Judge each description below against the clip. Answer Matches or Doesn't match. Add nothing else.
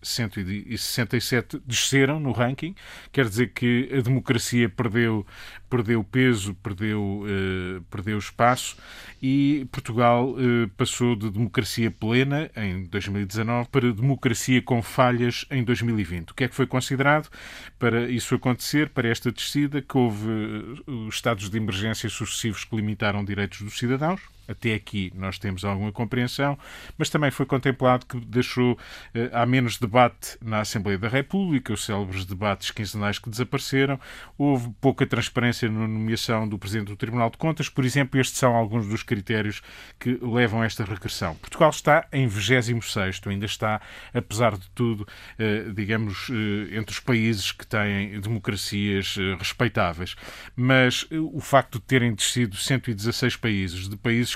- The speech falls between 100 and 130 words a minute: Doesn't match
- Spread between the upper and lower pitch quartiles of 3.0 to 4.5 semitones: Matches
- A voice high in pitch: Doesn't match